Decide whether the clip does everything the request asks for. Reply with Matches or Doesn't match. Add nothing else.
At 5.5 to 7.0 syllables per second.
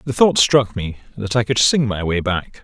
Doesn't match